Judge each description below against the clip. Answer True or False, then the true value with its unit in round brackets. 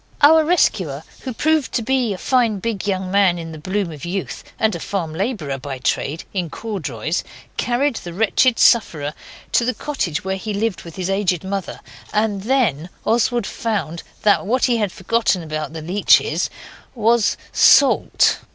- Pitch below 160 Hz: False (200 Hz)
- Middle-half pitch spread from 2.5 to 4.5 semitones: False (5.4 semitones)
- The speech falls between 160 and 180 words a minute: True (170 wpm)